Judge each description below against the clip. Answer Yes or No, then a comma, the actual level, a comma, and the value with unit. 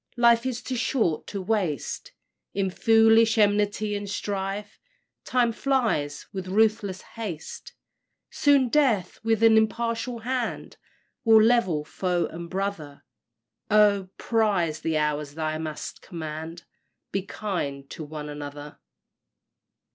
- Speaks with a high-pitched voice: Yes, high, 200 Hz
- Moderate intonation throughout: No, wide, 5.8 semitones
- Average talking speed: No, slow, 115 wpm